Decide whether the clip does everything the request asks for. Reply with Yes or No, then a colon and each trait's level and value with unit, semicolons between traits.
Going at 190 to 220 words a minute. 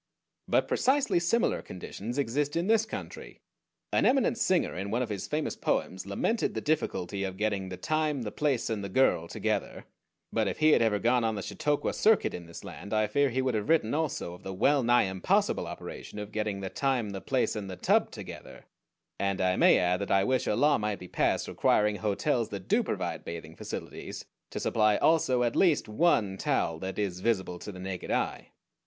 Yes: fast, 205 wpm